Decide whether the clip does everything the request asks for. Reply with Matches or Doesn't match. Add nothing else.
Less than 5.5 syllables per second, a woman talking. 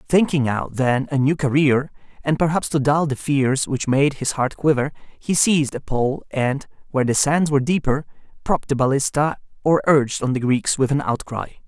Doesn't match